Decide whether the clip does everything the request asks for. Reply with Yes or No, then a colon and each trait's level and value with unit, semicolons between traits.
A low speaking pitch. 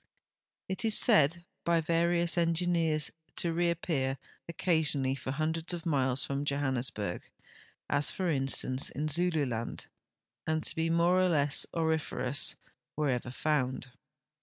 No: medium, 155 Hz